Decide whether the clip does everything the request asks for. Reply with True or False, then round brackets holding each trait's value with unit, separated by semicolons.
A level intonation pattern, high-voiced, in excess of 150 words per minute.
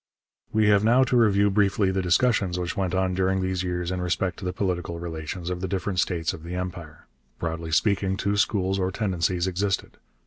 False (2.0 semitones; 95 Hz; 200 wpm)